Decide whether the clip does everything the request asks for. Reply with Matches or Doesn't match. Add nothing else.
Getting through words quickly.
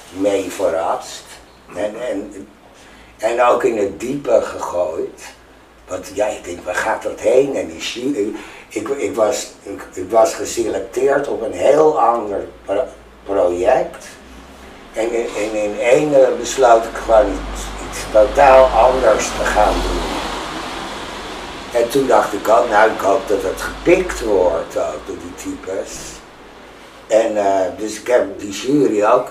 Doesn't match